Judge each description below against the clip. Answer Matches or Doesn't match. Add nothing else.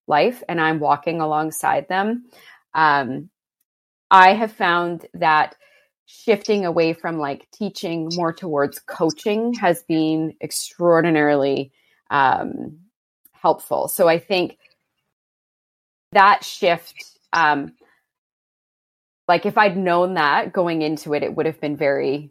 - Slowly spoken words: Matches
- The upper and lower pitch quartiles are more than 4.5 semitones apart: Doesn't match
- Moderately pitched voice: Matches